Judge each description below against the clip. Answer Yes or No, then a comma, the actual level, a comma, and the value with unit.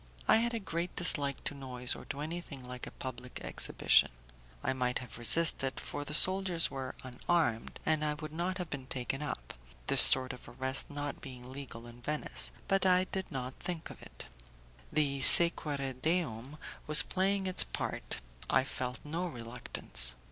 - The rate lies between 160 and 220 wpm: Yes, average, 170 wpm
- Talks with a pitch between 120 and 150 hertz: Yes, medium, 140 Hz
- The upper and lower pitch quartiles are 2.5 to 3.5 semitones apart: No, average, 4.9 semitones